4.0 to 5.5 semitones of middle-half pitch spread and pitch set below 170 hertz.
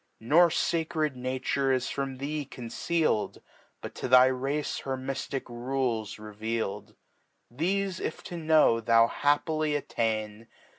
Yes: average, 4.9 semitones; low, 135 Hz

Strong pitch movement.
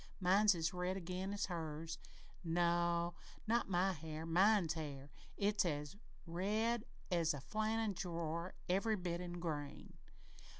No: average, 3.1 semitones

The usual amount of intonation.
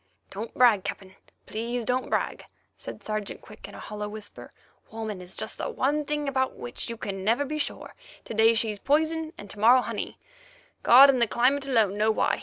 Yes: average, 4.6 semitones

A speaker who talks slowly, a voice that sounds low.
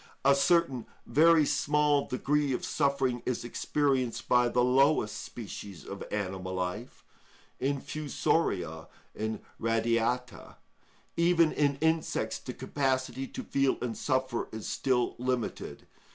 Yes: slow, 110 wpm; low, 130 Hz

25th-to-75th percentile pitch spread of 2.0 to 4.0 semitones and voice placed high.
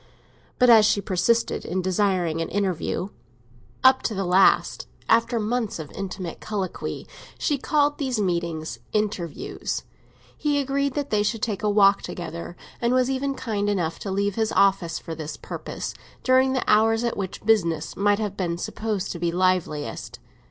No: average, 4.7 semitones; high, 200 Hz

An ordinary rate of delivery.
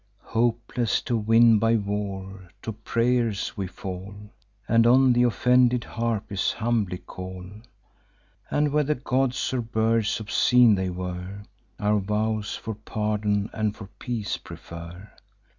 No: slow, 125 wpm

